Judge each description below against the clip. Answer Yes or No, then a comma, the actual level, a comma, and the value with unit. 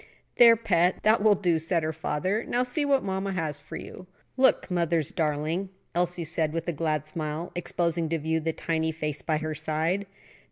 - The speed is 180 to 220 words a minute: Yes, average, 190 wpm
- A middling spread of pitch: Yes, average, 3.3 semitones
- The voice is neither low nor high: Yes, medium, 165 Hz